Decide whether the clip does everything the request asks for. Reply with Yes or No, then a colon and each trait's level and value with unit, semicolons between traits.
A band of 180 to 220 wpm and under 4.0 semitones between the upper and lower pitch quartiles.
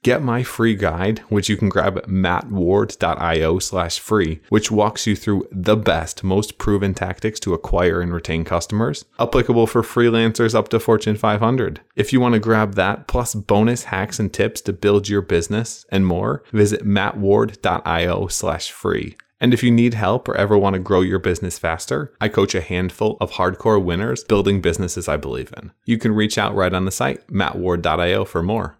Yes: average, 185 wpm; average, 3.0 semitones